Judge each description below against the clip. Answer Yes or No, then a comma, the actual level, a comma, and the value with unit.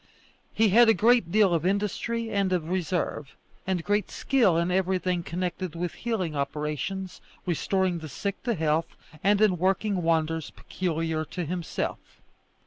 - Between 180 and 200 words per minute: No, average, 145 wpm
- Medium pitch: Yes, medium, 180 Hz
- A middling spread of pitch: Yes, average, 3.4 semitones